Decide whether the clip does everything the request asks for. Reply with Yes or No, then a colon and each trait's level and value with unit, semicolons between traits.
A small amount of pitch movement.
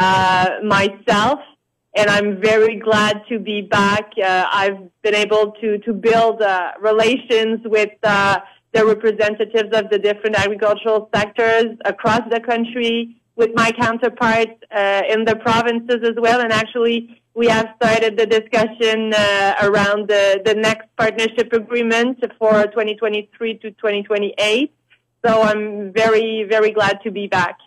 Yes: narrow, 1.6 semitones